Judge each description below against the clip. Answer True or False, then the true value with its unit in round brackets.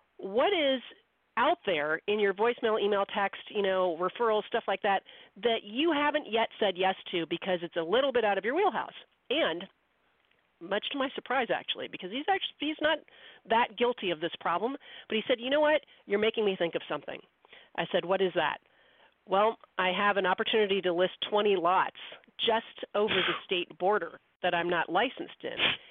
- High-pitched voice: True (205 Hz)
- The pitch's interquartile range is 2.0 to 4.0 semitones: False (4.4 semitones)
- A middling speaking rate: True (190 wpm)